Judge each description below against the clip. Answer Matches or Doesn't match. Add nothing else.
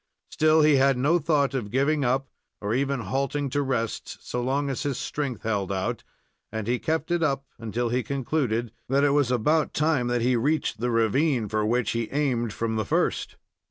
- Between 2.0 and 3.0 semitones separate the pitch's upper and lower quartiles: Doesn't match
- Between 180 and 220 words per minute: Matches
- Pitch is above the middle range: Doesn't match